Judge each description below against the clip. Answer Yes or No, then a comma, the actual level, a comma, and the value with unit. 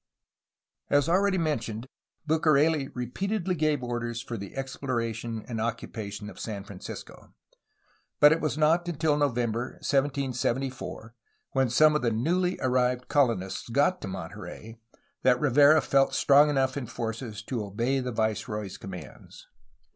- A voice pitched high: No, low, 125 Hz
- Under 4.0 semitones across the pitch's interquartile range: No, average, 4.5 semitones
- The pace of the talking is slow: Yes, slow, 130 wpm